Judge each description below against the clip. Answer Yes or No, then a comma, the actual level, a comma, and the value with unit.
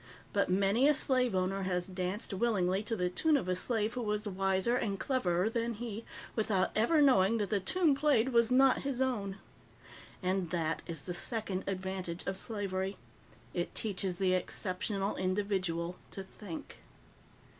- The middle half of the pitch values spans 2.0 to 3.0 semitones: No, average, 3.8 semitones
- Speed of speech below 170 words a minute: Yes, average, 160 wpm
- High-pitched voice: Yes, high, 195 Hz